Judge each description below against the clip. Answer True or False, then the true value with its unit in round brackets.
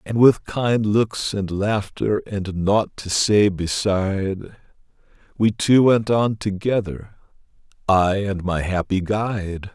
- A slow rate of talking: True (130 wpm)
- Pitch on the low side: True (100 Hz)